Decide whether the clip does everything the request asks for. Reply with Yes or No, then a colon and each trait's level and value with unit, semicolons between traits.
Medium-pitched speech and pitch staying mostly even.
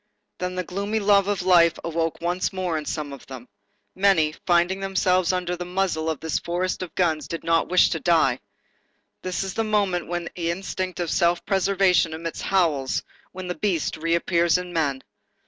Yes: medium, 175 Hz; narrow, 2.2 semitones